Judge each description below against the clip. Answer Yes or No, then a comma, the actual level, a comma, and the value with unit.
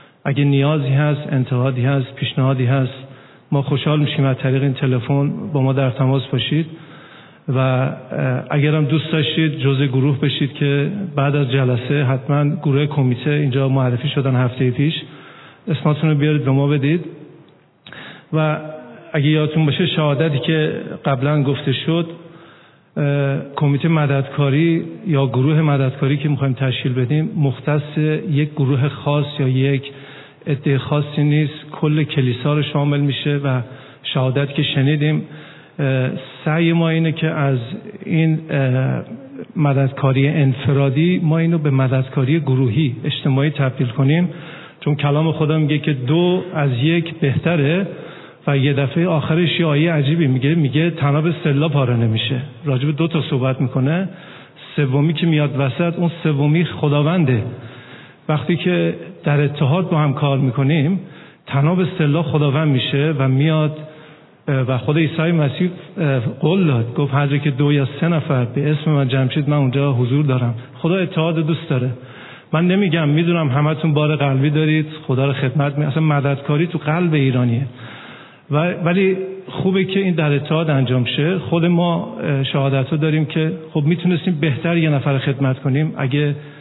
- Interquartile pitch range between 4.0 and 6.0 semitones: No, narrow, 2.6 semitones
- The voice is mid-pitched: Yes, medium, 145 Hz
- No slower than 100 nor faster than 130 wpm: No, average, 145 wpm